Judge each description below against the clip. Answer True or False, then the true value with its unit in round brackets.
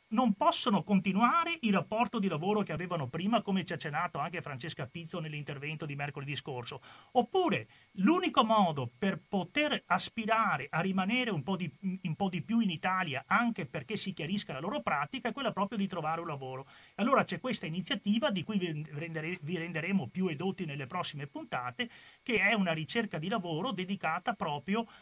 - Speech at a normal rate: False (180 wpm)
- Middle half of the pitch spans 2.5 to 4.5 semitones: False (5.2 semitones)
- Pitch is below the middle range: False (185 Hz)